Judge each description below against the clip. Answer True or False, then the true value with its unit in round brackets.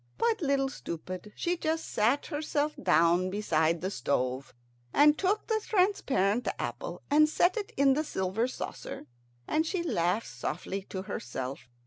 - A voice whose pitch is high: True (250 Hz)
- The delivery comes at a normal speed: True (145 wpm)